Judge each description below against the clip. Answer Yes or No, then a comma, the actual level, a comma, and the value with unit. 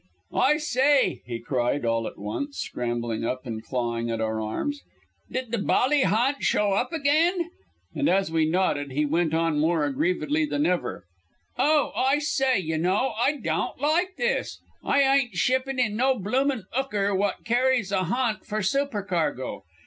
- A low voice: No, high, 210 Hz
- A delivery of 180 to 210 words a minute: No, average, 165 wpm